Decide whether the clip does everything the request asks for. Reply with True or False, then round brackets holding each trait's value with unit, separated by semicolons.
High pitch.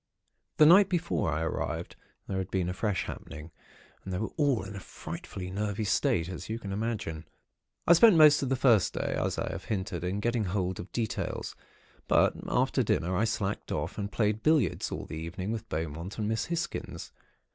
False (105 Hz)